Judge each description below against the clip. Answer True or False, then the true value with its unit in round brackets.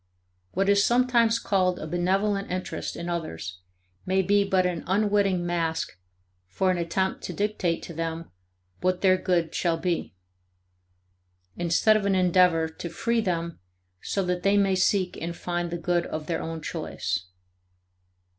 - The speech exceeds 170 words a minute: False (155 wpm)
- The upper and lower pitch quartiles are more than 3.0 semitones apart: False (2.7 semitones)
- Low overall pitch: False (180 Hz)